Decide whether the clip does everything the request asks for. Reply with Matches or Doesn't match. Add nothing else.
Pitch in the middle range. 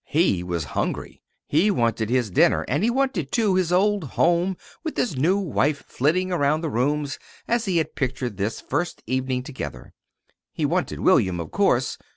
Matches